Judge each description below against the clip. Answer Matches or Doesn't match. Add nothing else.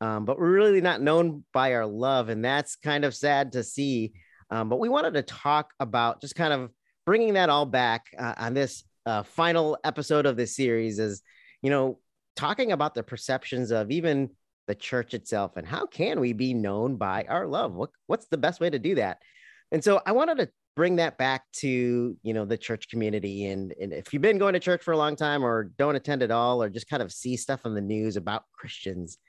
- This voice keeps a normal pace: Doesn't match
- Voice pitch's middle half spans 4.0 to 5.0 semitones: Matches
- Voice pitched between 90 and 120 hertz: Doesn't match